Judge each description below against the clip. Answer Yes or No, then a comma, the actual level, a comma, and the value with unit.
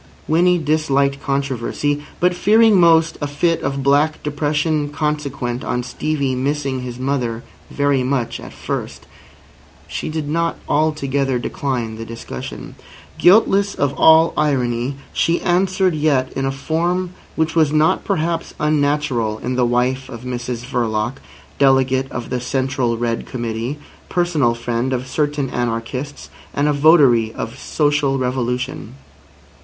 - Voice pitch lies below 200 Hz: Yes, medium, 140 Hz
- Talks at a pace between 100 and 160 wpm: Yes, slow, 135 wpm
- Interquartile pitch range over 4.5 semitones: No, average, 3.7 semitones